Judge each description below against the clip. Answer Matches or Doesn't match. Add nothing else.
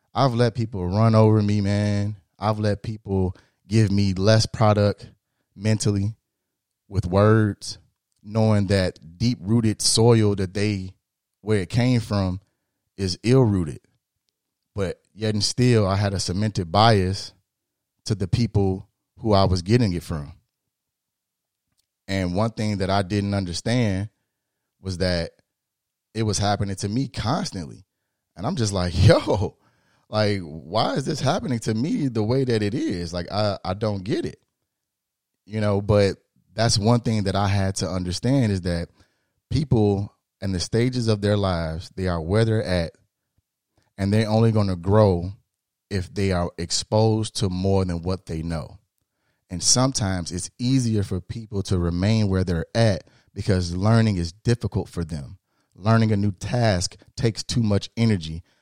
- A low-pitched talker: Matches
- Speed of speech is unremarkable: Matches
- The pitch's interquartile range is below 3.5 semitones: Matches